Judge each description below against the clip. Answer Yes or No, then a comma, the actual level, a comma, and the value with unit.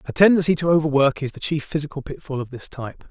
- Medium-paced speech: No, fast, 230 wpm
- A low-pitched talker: No, medium, 150 Hz